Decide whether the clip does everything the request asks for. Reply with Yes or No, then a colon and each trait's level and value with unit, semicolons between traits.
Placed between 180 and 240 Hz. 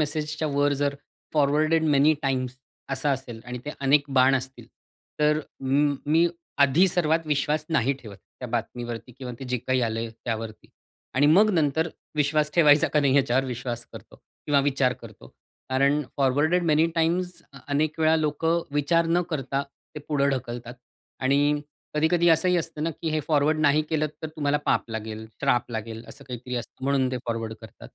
No: medium, 140 Hz